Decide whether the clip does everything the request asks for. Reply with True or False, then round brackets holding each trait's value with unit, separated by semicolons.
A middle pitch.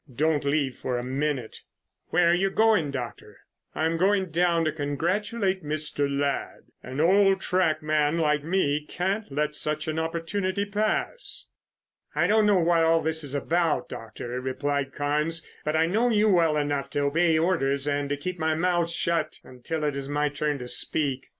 True (155 Hz)